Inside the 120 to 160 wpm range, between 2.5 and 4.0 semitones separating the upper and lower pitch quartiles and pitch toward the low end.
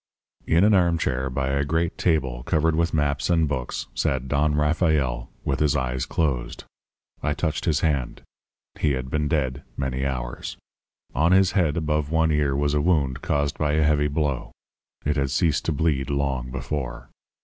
No: average, 170 wpm; average, 2.9 semitones; very low, 75 Hz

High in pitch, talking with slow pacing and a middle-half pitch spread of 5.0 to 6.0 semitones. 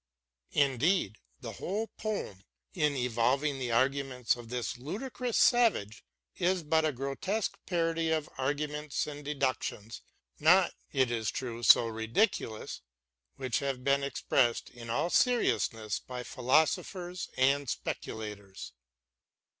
No: low, 135 Hz; slow, 120 wpm; average, 5.3 semitones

